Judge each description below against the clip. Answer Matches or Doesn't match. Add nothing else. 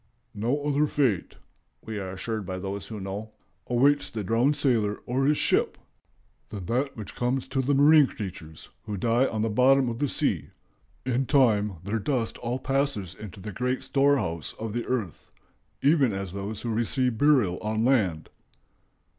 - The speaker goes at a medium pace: Matches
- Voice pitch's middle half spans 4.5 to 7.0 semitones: Matches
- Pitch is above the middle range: Doesn't match